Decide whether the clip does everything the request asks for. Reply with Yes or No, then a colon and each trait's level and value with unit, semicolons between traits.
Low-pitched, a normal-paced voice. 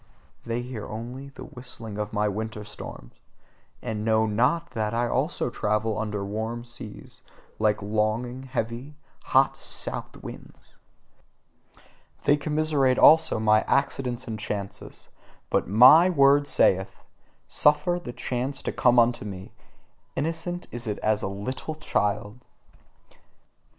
No: low, 120 Hz; slow, 125 wpm